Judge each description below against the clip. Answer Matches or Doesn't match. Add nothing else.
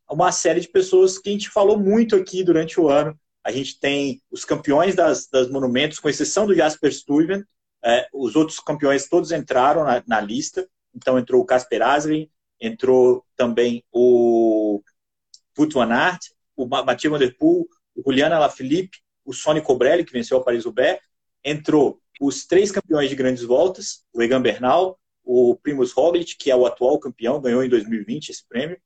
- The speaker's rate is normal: Matches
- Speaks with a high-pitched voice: Doesn't match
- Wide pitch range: Matches